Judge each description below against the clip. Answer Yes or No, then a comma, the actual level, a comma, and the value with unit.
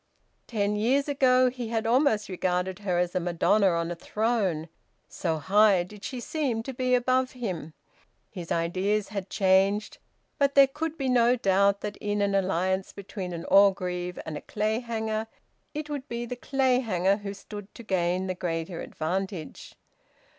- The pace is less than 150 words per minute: No, average, 160 wpm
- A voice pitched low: No, high, 205 Hz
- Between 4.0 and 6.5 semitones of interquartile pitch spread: Yes, average, 4.7 semitones